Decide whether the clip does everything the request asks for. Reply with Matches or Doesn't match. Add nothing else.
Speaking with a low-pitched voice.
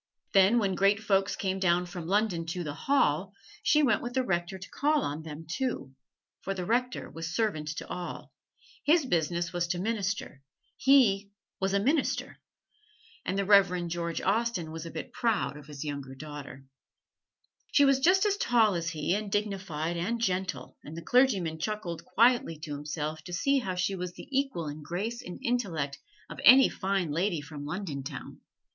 Doesn't match